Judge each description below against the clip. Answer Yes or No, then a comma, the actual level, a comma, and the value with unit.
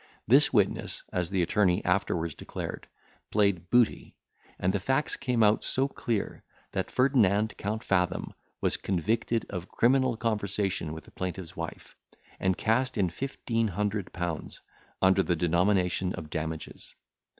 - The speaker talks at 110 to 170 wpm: Yes, average, 140 wpm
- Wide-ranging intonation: No, average, 4.2 semitones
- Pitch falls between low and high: No, low, 100 Hz